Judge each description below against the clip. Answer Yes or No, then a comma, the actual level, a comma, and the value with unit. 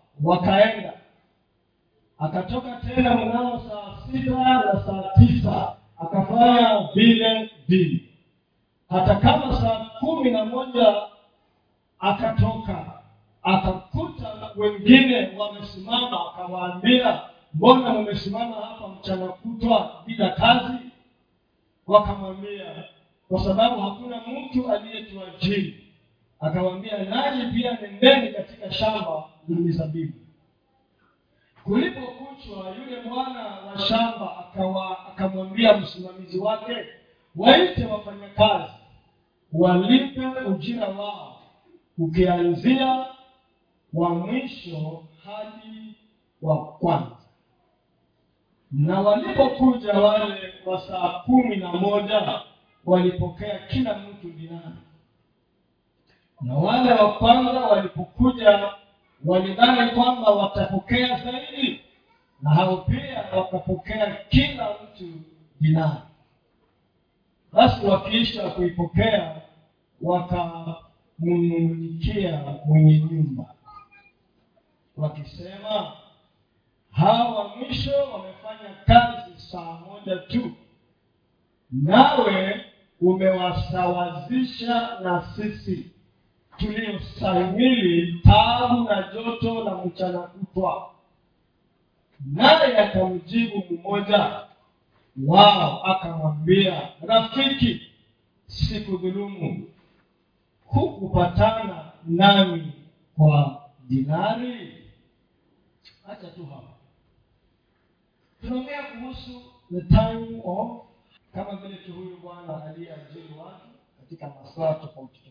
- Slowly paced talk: Yes, slow, 75 wpm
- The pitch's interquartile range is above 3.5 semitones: Yes, average, 4.8 semitones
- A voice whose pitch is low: No, high, 195 Hz